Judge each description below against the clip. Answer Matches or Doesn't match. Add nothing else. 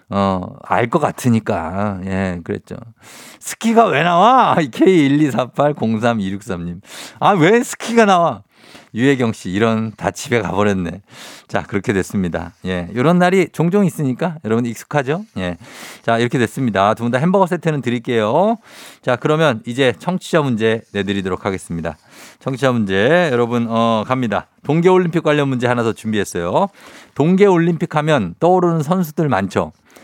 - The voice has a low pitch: Matches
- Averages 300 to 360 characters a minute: Matches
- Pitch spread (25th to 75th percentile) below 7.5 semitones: Doesn't match